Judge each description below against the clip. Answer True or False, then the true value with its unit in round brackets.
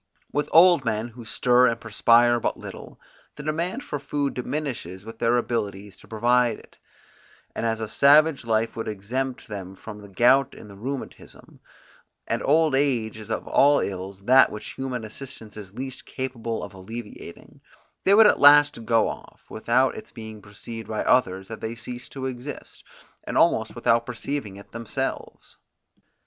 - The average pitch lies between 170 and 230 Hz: False (115 Hz)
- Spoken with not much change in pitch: False (3.6 semitones)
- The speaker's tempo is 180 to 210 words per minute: False (165 wpm)